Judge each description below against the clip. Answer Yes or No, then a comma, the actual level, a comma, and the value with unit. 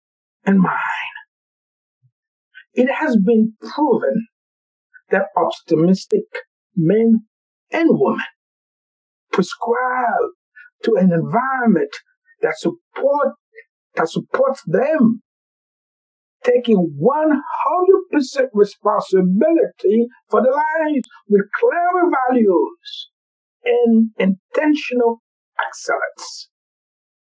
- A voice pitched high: Yes, very high, 265 Hz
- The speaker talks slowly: Yes, slow, 75 wpm